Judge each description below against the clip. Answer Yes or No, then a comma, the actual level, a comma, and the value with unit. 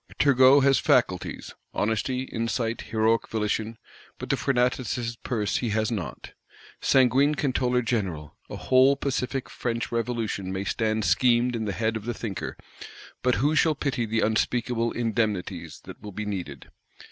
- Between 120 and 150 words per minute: Yes, average, 145 wpm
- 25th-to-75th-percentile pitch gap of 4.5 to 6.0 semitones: No, average, 2.8 semitones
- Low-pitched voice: Yes, low, 115 Hz